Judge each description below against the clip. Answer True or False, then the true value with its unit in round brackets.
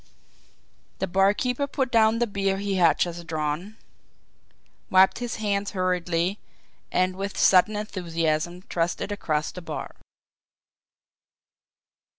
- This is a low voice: False (190 Hz)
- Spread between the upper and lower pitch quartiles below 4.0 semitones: True (3.1 semitones)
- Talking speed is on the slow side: True (115 wpm)